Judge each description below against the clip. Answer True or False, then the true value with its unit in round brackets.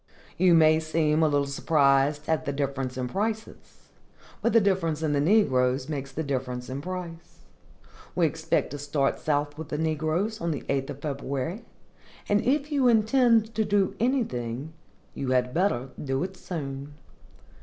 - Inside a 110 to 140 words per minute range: False (160 wpm)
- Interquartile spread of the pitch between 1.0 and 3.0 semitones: False (5.4 semitones)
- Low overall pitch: False (155 Hz)